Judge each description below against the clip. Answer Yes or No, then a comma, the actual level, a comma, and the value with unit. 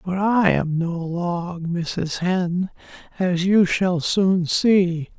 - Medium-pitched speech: Yes, medium, 180 Hz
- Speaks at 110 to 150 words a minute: Yes, average, 140 wpm